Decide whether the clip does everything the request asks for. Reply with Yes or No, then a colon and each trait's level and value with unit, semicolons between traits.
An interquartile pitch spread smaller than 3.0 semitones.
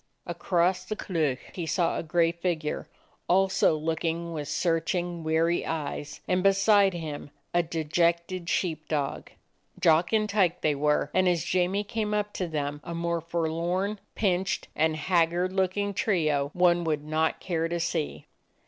Yes: narrow, 2.5 semitones